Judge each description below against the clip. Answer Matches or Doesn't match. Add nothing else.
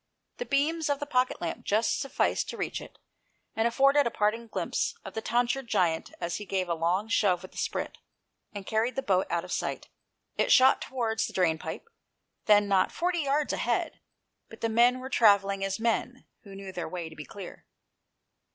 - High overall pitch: Matches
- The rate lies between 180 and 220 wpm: Matches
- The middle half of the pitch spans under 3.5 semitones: Doesn't match